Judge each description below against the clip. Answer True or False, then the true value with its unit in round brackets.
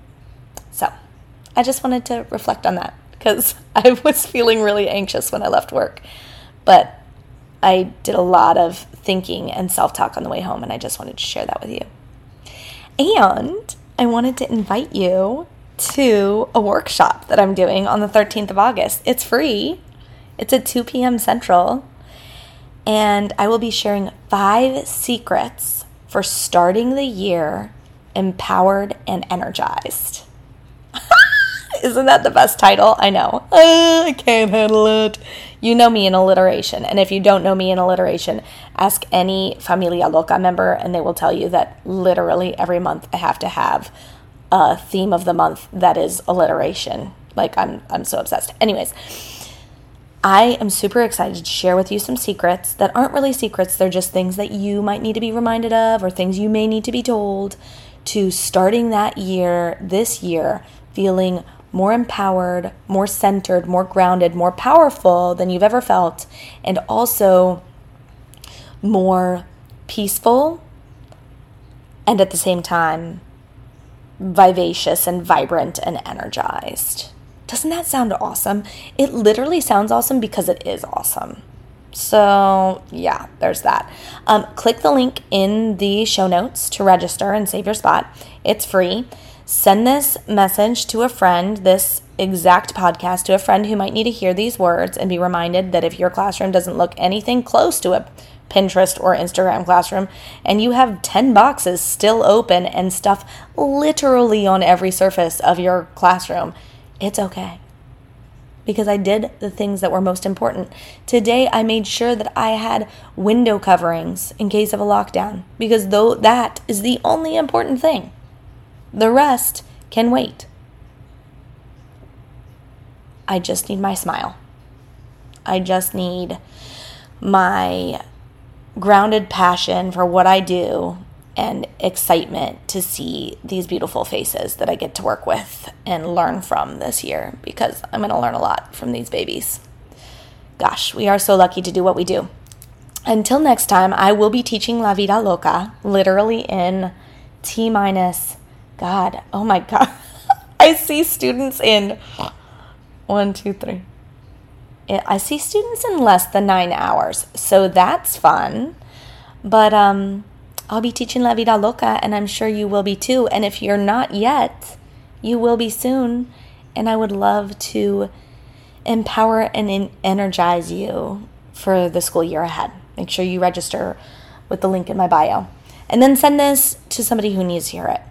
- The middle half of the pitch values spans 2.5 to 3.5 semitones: False (4.2 semitones)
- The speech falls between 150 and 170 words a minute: True (160 wpm)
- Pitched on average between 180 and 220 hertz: True (190 Hz)